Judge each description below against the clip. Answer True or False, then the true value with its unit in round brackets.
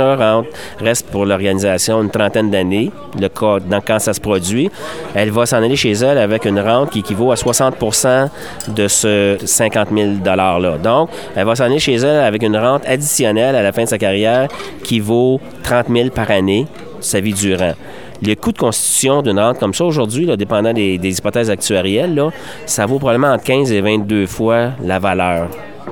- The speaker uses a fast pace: False (190 wpm)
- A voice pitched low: True (110 Hz)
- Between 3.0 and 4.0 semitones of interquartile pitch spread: True (3.5 semitones)